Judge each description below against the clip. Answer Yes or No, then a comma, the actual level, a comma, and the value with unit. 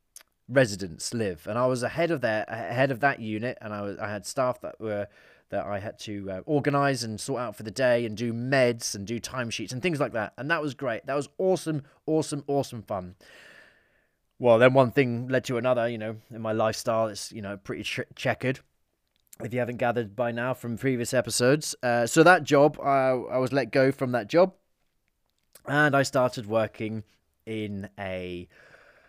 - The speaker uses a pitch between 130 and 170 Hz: No, low, 120 Hz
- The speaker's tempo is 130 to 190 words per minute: No, average, 200 wpm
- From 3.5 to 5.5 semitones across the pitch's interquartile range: Yes, average, 3.9 semitones